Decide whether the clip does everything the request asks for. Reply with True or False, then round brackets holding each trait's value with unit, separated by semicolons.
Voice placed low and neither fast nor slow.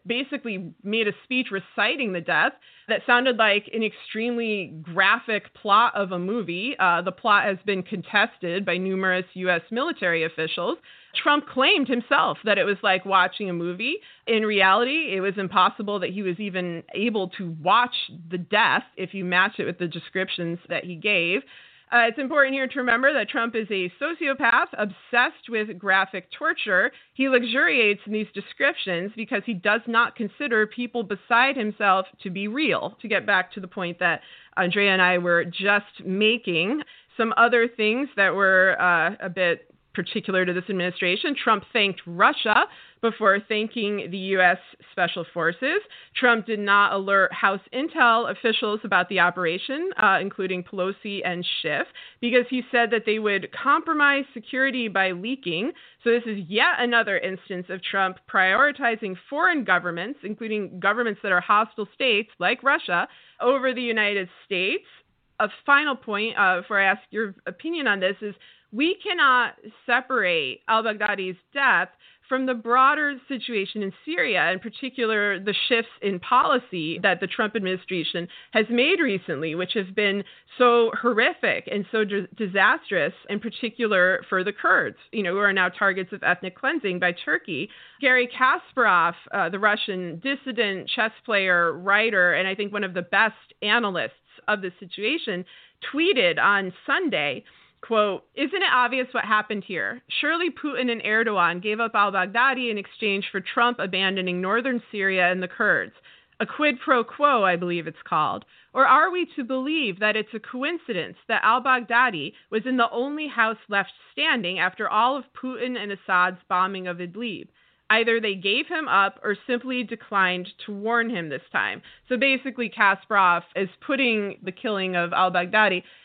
False (210 Hz; 165 wpm)